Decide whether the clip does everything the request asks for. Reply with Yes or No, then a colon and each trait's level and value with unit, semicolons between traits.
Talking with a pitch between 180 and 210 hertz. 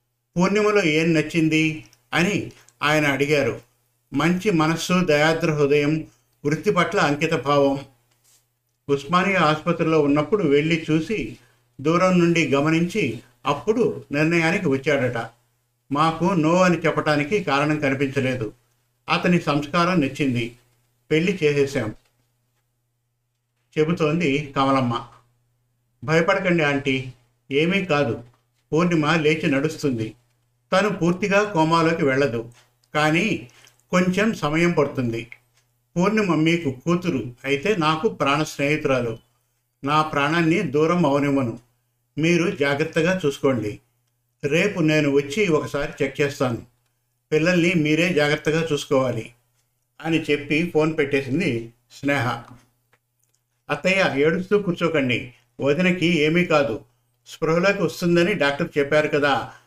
No: medium, 145 Hz